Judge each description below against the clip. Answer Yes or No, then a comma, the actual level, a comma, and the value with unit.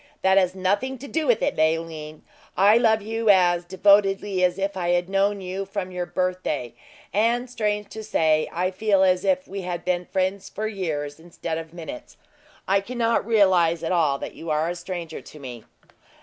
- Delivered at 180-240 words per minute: Yes, average, 190 wpm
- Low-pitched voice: No, medium, 185 Hz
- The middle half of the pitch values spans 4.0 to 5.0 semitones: No, average, 3.1 semitones